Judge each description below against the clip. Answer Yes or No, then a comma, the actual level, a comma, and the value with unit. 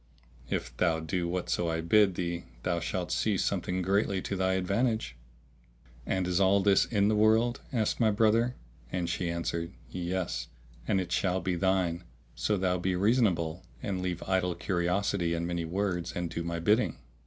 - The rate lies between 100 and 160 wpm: No, average, 170 wpm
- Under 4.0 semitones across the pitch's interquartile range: Yes, average, 2.7 semitones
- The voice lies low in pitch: Yes, very low, 90 Hz